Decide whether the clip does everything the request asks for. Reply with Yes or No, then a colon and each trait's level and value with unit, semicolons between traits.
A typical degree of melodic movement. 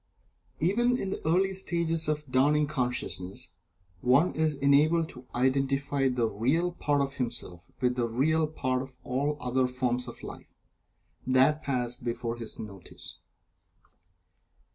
Yes: average, 3.6 semitones